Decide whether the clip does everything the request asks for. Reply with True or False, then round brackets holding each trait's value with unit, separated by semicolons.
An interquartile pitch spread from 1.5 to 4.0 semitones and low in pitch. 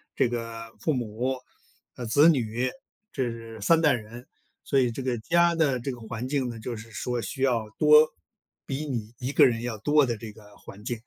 True (3.1 semitones; 120 Hz)